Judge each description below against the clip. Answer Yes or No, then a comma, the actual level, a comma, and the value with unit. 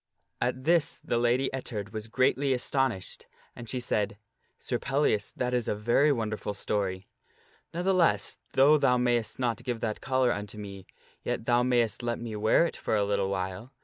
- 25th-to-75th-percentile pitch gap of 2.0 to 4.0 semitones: Yes, average, 3.7 semitones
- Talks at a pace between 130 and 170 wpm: No, average, 180 wpm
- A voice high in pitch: No, low, 120 Hz